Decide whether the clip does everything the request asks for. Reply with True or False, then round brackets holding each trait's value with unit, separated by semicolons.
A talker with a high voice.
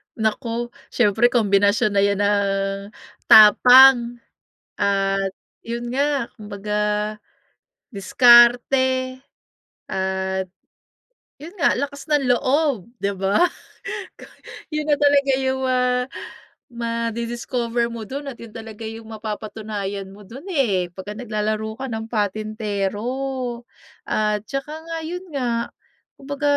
True (230 Hz)